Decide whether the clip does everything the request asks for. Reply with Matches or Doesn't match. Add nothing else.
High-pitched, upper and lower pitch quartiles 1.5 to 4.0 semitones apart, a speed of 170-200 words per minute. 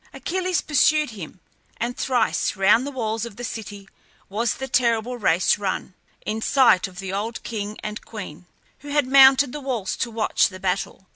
Doesn't match